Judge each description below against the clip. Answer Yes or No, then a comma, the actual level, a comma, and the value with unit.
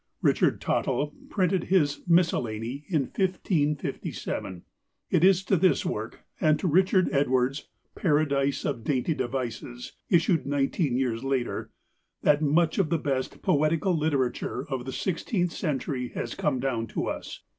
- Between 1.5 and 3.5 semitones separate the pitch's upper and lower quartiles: No, average, 4.5 semitones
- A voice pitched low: No, medium, 145 Hz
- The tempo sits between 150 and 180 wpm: No, slow, 135 wpm